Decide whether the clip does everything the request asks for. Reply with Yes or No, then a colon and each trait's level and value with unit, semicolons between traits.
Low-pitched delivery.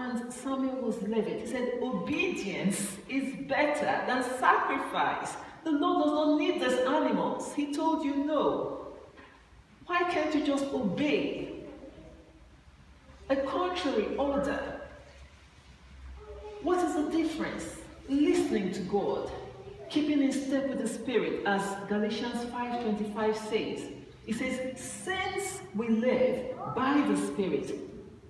No: very high, 255 Hz